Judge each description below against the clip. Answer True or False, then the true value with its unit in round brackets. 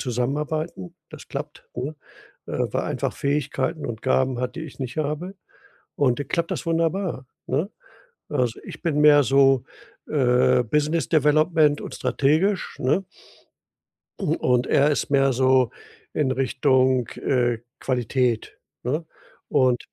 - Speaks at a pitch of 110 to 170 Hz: True (135 Hz)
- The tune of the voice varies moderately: True (3.3 semitones)